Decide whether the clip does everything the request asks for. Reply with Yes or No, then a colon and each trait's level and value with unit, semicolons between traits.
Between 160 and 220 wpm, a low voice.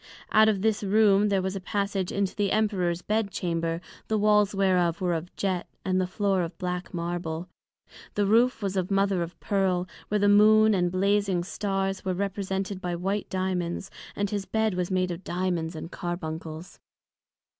No: average, 175 wpm; high, 190 Hz